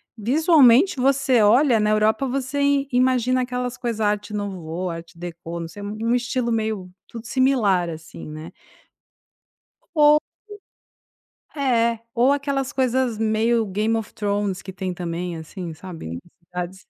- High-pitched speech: Yes, high, 220 Hz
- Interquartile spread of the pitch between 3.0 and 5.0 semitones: No, wide, 5.4 semitones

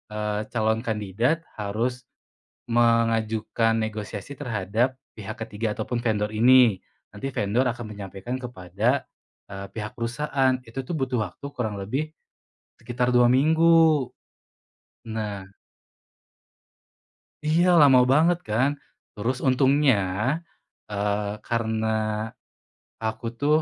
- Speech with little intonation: No, average, 3.5 semitones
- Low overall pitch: Yes, low, 115 Hz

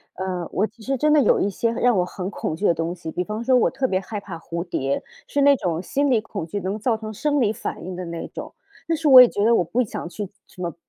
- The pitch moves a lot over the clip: Yes, wide, 5.7 semitones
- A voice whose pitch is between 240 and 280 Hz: No, high, 205 Hz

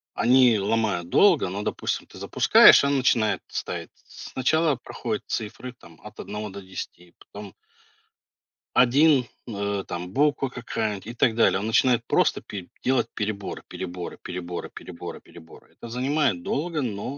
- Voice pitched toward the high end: No, low, 110 Hz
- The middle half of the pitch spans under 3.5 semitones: No, average, 4.8 semitones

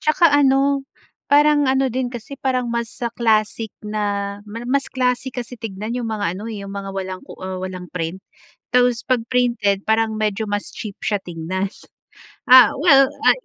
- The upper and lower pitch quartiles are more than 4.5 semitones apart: No, average, 4.2 semitones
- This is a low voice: No, high, 225 Hz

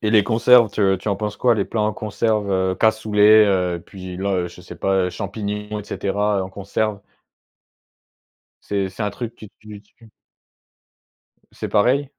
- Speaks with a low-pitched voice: Yes, low, 105 Hz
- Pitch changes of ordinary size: No, narrow, 1.9 semitones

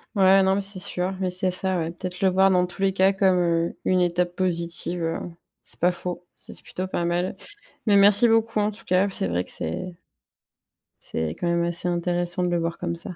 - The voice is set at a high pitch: No, medium, 180 Hz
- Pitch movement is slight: Yes, narrow, 1.7 semitones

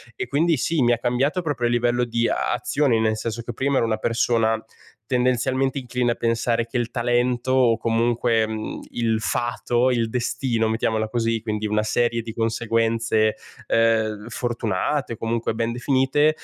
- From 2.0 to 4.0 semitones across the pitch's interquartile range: No, narrow, 1.6 semitones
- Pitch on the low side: Yes, low, 115 Hz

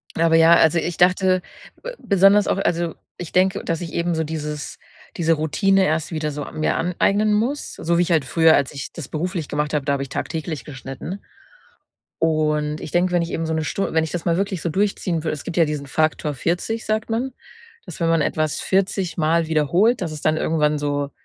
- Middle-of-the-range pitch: Yes, medium, 165 Hz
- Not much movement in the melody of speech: No, average, 3.0 semitones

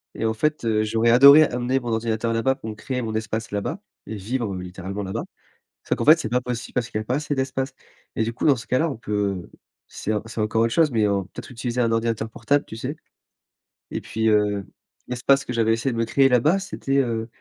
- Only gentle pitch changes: No, average, 3.2 semitones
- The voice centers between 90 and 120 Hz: Yes, low, 115 Hz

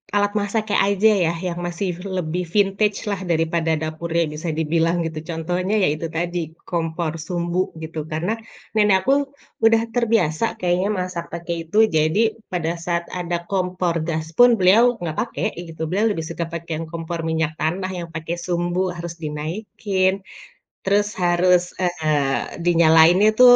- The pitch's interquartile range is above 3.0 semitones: No, narrow, 2.6 semitones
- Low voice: No, medium, 175 Hz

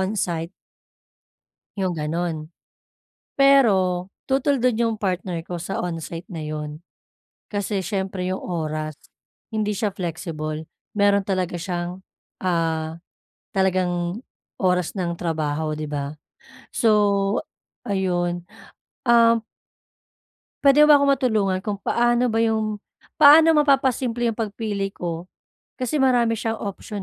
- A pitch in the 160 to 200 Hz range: Yes, high, 190 Hz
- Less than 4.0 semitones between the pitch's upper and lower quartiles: No, average, 4.7 semitones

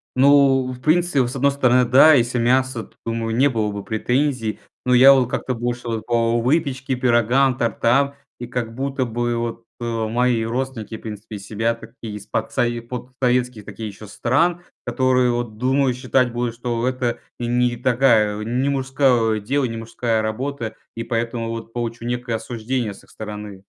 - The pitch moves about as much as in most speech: No, narrow, 2.2 semitones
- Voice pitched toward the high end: No, low, 120 Hz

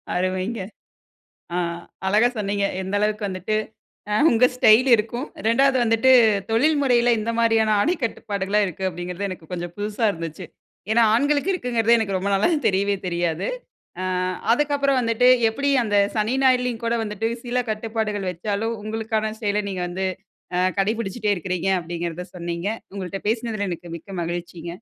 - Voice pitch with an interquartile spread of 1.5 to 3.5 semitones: No, average, 3.9 semitones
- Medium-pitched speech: No, high, 210 Hz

